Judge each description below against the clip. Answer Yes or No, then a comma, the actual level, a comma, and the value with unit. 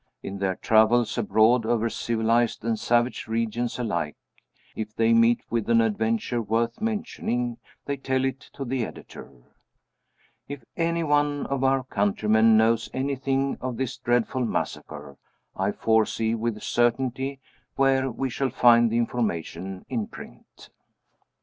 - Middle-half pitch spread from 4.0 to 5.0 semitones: No, average, 3.0 semitones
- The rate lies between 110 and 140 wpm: Yes, slow, 135 wpm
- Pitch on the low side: Yes, low, 115 Hz